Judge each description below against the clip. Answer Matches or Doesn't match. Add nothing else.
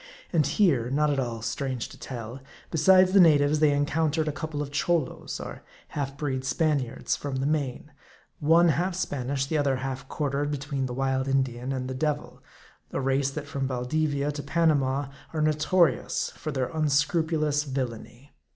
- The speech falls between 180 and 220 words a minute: Doesn't match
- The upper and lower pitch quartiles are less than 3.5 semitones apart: Matches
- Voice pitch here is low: Doesn't match